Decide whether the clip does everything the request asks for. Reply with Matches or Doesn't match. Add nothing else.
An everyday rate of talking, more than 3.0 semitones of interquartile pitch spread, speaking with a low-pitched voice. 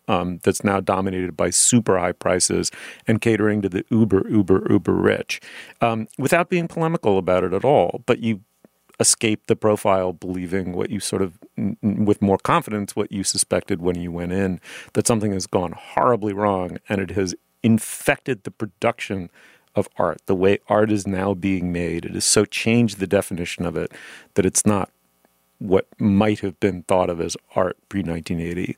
Doesn't match